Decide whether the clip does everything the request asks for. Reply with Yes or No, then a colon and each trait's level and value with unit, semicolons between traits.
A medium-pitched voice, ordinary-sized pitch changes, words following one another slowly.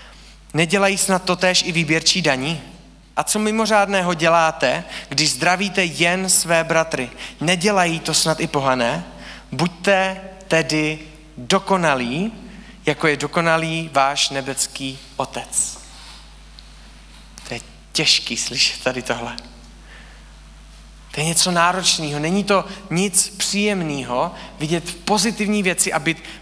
Yes: medium, 165 Hz; average, 4.5 semitones; slow, 110 wpm